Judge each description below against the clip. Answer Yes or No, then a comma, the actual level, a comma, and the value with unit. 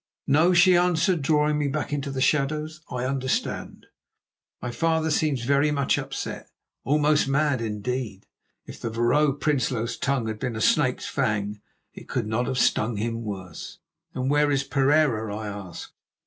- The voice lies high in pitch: No, low, 135 Hz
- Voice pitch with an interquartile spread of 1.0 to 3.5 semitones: No, average, 4.5 semitones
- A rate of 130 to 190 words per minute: Yes, average, 160 wpm